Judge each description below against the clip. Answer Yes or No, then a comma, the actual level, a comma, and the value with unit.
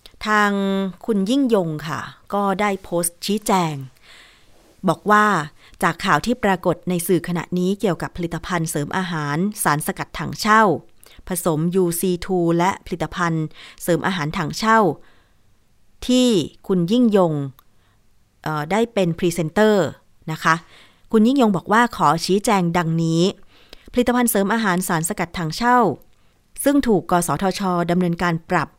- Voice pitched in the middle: Yes, medium, 180 Hz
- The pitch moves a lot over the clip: No, average, 4.2 semitones